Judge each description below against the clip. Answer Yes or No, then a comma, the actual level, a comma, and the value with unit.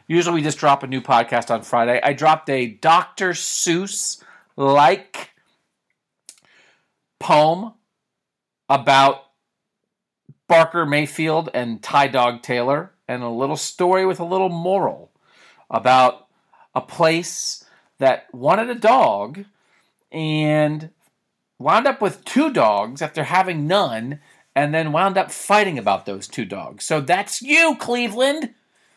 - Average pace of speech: No, slow, 125 wpm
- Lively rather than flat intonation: Yes, wide, 6.3 semitones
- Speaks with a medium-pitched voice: Yes, medium, 160 Hz